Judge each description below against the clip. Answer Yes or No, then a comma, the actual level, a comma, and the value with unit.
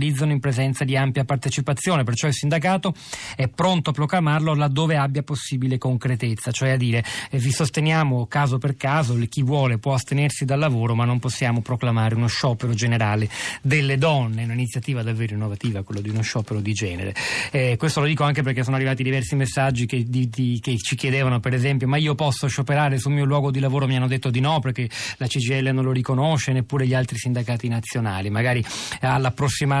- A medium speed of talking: No, fast, 190 wpm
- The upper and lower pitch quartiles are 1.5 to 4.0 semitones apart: Yes, average, 2.8 semitones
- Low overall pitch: Yes, low, 130 Hz